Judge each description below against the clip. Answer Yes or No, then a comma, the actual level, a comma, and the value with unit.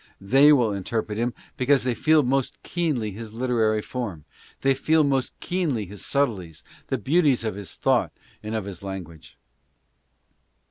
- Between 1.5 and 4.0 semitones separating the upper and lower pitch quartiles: No, average, 4.9 semitones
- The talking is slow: No, average, 150 wpm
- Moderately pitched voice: No, low, 120 Hz